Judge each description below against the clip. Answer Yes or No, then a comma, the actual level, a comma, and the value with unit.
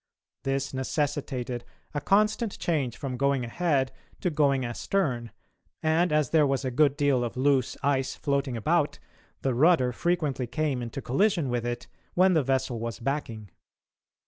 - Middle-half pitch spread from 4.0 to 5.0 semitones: No, average, 3.5 semitones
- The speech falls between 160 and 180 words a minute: No, average, 150 wpm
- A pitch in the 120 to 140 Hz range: Yes, low, 135 Hz